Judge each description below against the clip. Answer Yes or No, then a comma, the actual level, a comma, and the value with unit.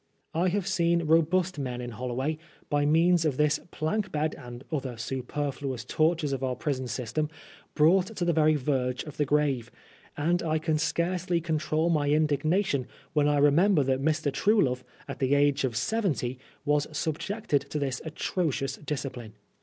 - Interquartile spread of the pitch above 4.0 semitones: No, average, 3.7 semitones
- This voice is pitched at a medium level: Yes, medium, 150 Hz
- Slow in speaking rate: No, average, 160 wpm